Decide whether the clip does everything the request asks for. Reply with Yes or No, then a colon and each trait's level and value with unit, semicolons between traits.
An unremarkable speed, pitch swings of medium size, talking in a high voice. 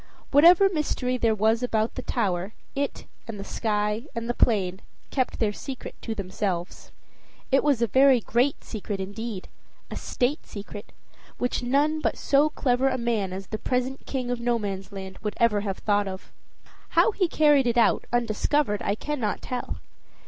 Yes: average, 165 wpm; average, 4.3 semitones; high, 235 Hz